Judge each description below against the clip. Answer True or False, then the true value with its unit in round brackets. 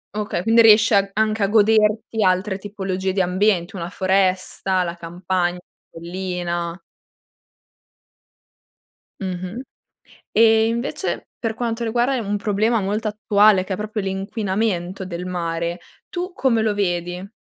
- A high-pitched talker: True (195 Hz)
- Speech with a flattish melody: False (3.1 semitones)